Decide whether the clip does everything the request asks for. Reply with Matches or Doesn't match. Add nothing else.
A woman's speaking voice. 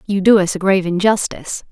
Matches